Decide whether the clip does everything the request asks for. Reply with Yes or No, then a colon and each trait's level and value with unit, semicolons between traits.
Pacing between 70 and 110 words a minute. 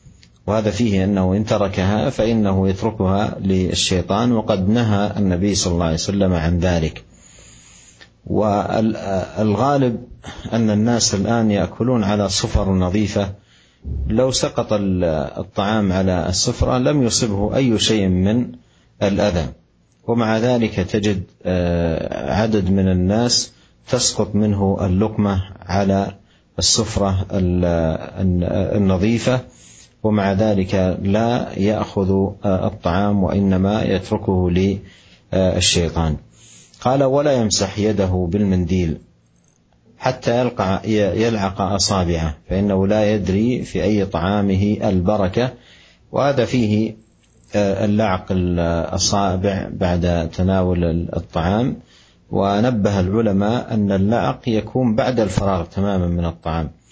Yes: average, 95 wpm